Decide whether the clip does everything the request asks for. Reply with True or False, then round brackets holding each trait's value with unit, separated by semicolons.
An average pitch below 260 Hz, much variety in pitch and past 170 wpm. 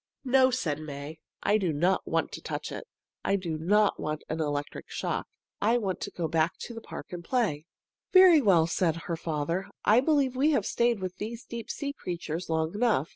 True (185 Hz; 6.7 semitones; 190 wpm)